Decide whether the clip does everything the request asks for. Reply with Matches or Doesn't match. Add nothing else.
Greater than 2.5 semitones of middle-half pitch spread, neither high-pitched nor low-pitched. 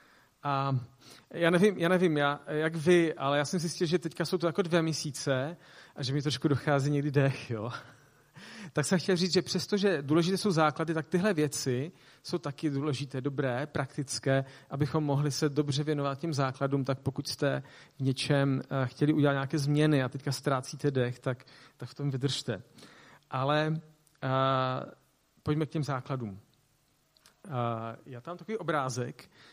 Matches